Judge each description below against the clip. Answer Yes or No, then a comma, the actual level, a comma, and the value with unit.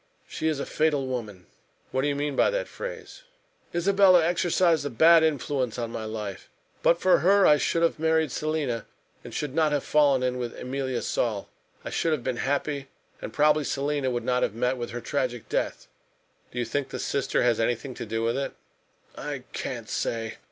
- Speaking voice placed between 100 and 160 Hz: Yes, medium, 140 Hz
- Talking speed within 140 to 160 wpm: No, average, 195 wpm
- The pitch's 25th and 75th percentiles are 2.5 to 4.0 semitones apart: No, average, 4.6 semitones